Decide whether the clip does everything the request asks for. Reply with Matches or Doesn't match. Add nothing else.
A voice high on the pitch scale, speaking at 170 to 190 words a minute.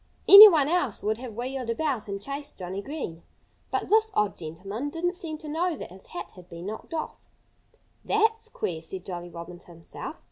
Matches